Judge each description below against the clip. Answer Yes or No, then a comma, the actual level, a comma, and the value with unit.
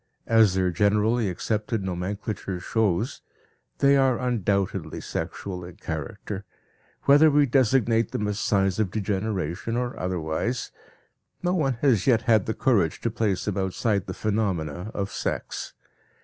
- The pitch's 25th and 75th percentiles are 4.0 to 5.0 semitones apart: No, average, 3.6 semitones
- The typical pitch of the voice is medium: No, low, 105 Hz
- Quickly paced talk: No, slow, 135 wpm